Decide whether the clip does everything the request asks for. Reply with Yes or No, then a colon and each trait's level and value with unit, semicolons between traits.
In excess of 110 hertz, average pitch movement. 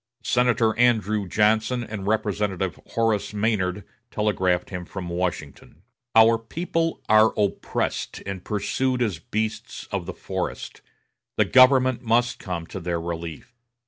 No: low, 105 Hz; average, 3.8 semitones